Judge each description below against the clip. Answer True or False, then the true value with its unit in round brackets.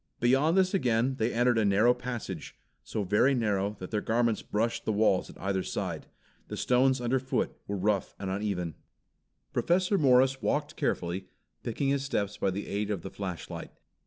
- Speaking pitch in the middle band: False (110 Hz)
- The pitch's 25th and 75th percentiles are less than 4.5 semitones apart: False (4.8 semitones)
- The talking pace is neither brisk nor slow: True (170 wpm)